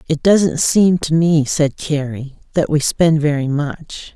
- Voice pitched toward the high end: No, medium, 155 Hz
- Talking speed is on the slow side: No, average, 175 wpm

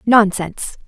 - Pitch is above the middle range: Yes, high, 205 Hz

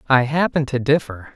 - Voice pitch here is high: No, low, 135 Hz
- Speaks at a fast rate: No, average, 175 wpm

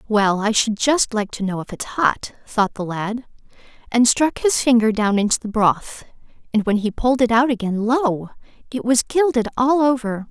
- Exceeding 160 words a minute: Yes, average, 200 wpm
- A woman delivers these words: Yes, female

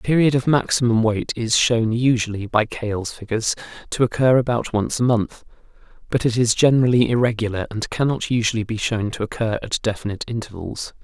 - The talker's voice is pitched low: Yes, low, 115 Hz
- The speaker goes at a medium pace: Yes, average, 175 wpm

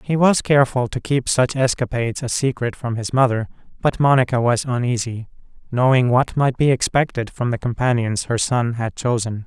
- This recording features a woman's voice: No, male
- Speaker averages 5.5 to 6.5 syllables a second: No, 5.2 syllables/s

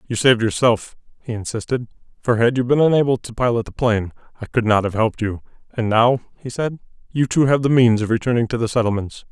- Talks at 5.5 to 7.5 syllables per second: Yes, 6.3 syllables/s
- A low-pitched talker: Yes, low, 120 Hz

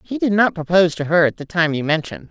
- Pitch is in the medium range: Yes, medium, 175 Hz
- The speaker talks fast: Yes, fast, 285 wpm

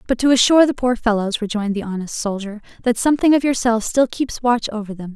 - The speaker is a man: No, female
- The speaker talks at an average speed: No, fast, 220 wpm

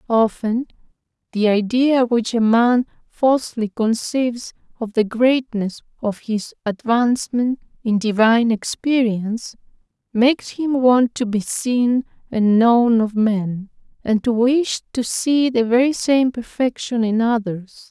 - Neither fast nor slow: No, slow, 125 wpm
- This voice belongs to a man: No, female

